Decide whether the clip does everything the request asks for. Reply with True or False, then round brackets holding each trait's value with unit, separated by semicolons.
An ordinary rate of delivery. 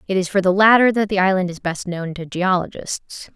False (230 wpm)